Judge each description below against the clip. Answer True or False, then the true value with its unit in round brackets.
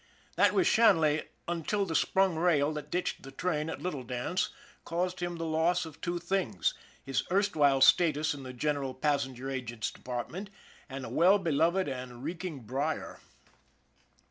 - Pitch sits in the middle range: True (155 Hz)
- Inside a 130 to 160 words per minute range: True (155 wpm)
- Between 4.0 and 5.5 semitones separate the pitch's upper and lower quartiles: True (4.7 semitones)